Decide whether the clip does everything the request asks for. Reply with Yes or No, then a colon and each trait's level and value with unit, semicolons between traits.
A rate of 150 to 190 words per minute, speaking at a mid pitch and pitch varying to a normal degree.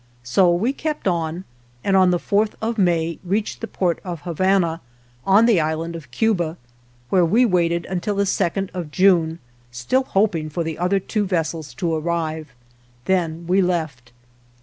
Yes: average, 165 wpm; medium, 175 Hz; average, 3.2 semitones